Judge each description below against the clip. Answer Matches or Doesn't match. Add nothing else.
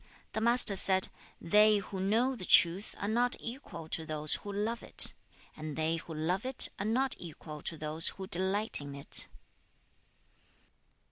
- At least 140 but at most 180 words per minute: Matches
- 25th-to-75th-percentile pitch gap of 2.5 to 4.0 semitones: Doesn't match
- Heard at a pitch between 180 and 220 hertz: Matches